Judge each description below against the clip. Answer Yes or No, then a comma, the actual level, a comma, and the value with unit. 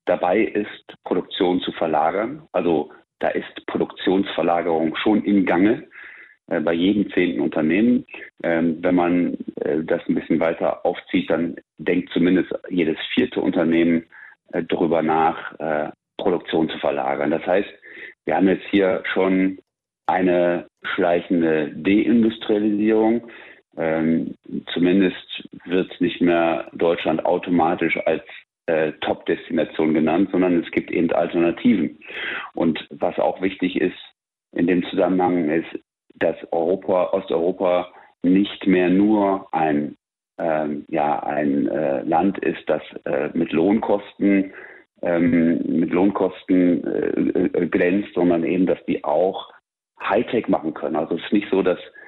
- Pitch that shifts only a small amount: Yes, narrow, 2.3 semitones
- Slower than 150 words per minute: Yes, slow, 125 wpm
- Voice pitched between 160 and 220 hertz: No, very low, 90 Hz